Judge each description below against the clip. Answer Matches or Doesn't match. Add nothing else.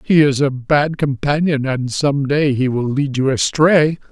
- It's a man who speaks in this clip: Matches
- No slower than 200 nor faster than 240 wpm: Doesn't match